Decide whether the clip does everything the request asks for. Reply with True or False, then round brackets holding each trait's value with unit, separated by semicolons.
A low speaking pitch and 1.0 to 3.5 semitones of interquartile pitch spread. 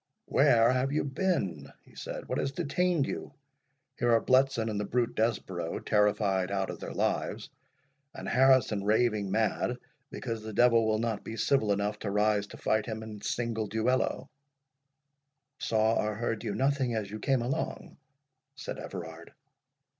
True (110 Hz; 3.2 semitones)